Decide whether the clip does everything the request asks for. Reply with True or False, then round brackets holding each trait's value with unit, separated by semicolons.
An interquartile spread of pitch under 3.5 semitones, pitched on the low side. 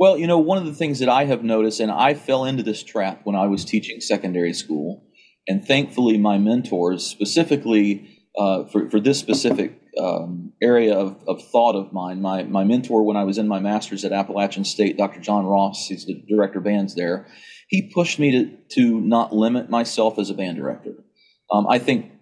False (4.4 semitones; 110 Hz)